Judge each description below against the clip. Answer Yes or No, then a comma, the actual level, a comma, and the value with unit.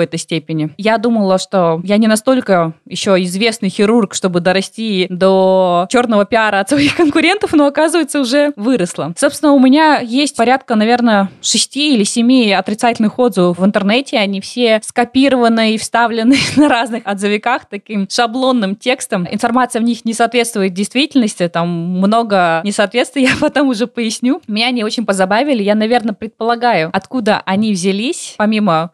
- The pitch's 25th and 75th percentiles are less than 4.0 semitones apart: No, average, 4.6 semitones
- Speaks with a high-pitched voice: Yes, high, 225 Hz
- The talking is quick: No, average, 150 wpm